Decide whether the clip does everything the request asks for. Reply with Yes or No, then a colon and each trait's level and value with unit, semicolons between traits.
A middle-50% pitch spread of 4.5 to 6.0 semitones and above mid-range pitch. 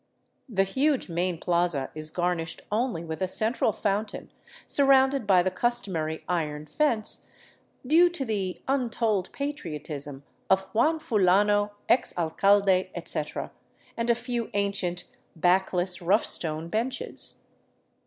Yes: wide, 5.5 semitones; high, 195 Hz